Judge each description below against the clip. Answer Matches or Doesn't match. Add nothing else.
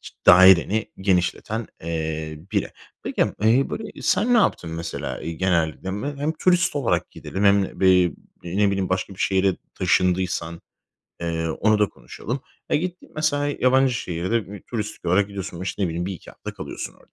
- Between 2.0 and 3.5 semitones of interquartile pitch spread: Doesn't match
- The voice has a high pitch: Doesn't match